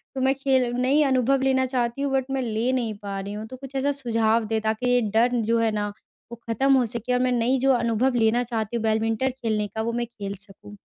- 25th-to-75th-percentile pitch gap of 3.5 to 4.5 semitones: No, average, 3.0 semitones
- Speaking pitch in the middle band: No, high, 235 Hz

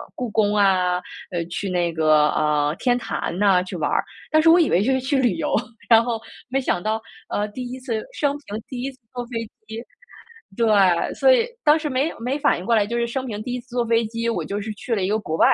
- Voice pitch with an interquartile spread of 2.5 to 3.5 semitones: No, average, 4.6 semitones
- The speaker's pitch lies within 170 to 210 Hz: No, high, 230 Hz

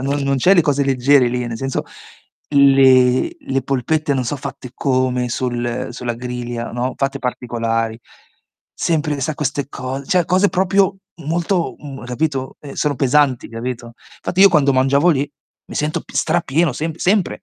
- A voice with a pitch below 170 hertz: Yes, low, 135 Hz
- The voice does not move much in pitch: No, average, 3.5 semitones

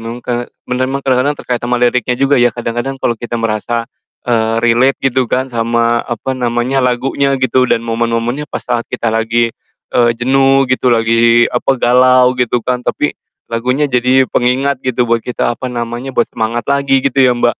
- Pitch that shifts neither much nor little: No, narrow, 1.6 semitones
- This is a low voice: Yes, low, 125 Hz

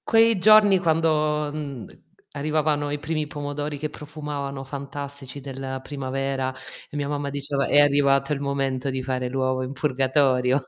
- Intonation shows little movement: Yes, narrow, 1.8 semitones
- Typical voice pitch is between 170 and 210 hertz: No, medium, 140 Hz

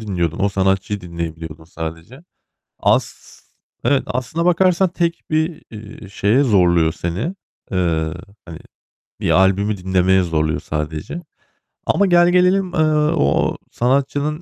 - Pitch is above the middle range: No, low, 100 Hz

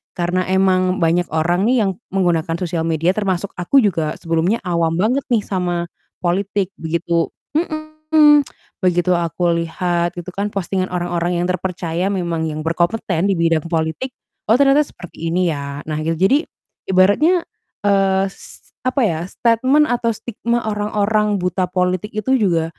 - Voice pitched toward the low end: No, medium, 185 Hz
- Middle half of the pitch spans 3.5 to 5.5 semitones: Yes, average, 3.8 semitones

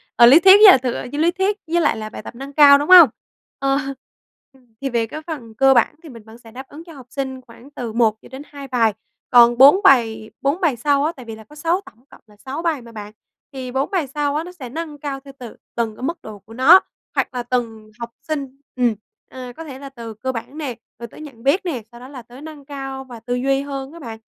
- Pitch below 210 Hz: No, very high, 265 Hz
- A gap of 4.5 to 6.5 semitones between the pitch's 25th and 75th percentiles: No, average, 3.7 semitones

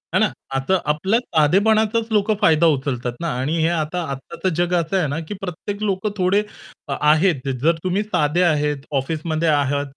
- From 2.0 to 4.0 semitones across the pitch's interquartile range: No, average, 4.5 semitones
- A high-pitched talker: No, medium, 165 Hz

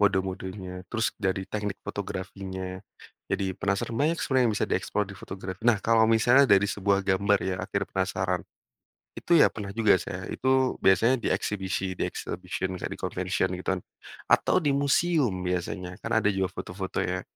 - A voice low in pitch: Yes, very low, 95 Hz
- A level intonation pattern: No, average, 3.0 semitones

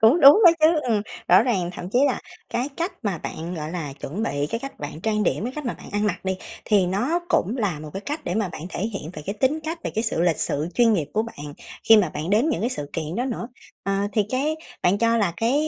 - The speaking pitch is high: Yes, high, 210 Hz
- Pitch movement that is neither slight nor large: No, wide, 6.0 semitones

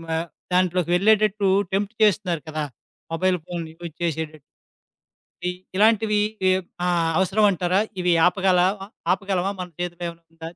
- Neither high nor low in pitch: Yes, medium, 180 Hz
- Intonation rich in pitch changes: No, average, 2.7 semitones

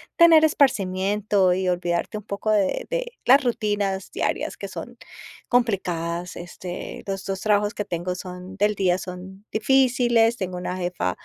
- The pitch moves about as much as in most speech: Yes, average, 3.4 semitones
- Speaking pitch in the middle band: No, high, 195 Hz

